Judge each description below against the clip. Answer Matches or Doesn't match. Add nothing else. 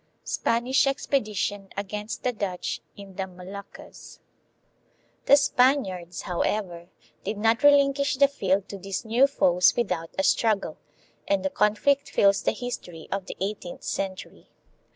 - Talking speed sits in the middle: Doesn't match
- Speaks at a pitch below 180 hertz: Doesn't match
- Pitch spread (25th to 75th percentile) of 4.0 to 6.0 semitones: Matches